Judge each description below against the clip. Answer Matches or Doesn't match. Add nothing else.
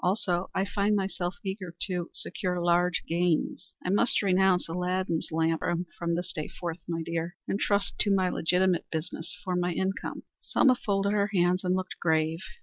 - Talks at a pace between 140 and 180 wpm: Matches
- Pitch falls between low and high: Matches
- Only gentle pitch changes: Matches